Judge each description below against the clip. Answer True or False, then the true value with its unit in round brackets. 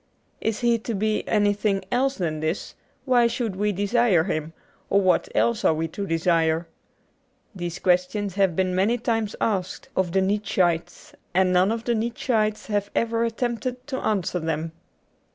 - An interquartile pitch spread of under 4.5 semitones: True (4.1 semitones)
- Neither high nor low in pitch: False (200 Hz)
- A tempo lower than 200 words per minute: True (165 wpm)